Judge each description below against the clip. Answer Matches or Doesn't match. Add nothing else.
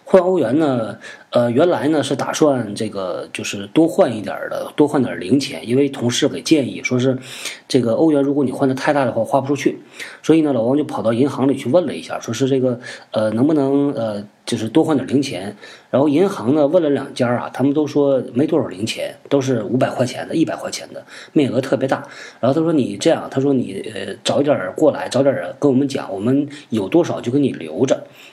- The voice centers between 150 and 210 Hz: Doesn't match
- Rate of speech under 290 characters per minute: Doesn't match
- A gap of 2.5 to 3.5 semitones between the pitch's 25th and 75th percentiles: Matches